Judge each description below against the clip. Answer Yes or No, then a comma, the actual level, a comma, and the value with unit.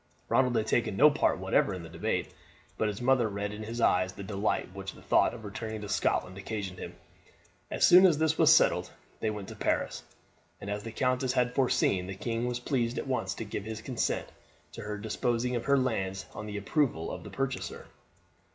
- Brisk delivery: Yes, fast, 210 wpm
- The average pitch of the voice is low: Yes, low, 110 Hz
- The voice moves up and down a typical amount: Yes, average, 3.9 semitones